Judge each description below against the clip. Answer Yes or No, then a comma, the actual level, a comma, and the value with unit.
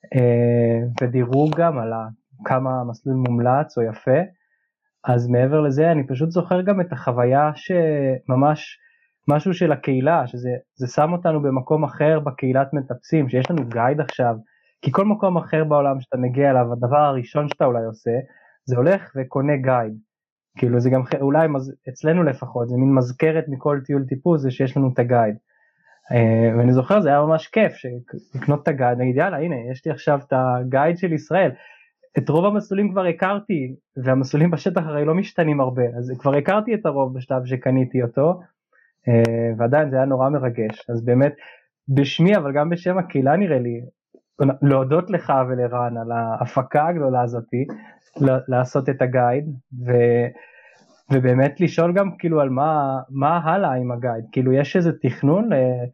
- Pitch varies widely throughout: No, average, 4.1 semitones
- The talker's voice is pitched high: No, low, 135 Hz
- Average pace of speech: No, fast, 160 wpm